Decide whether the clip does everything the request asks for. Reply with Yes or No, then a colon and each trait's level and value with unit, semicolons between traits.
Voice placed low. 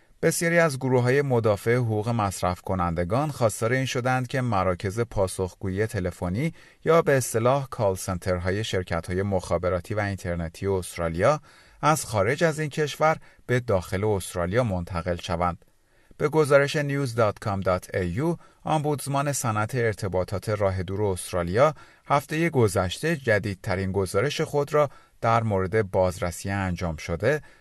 Yes: low, 105 Hz